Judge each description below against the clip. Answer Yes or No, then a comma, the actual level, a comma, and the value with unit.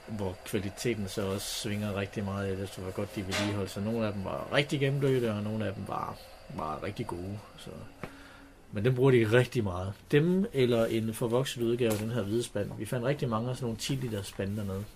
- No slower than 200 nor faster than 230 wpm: Yes, fast, 225 wpm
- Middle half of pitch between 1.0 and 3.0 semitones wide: No, average, 3.8 semitones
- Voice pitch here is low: Yes, low, 110 Hz